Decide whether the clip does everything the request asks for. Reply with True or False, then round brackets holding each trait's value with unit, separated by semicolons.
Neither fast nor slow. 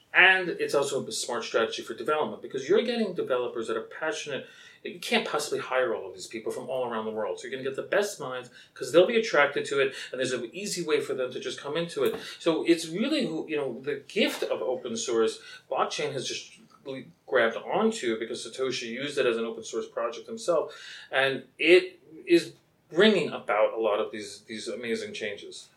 False (215 wpm)